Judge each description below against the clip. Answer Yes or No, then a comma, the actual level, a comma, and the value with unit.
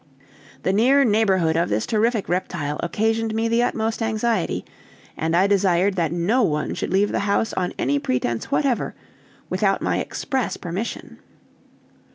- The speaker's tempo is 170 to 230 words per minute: No, average, 150 wpm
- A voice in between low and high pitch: No, high, 200 Hz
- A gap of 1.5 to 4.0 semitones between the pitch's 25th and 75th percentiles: No, average, 4.8 semitones